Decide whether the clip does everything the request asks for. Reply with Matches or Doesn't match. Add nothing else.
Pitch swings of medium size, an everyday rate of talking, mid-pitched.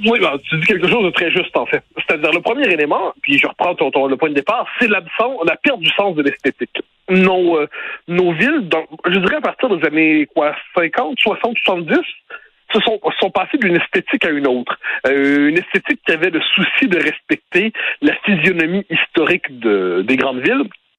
Doesn't match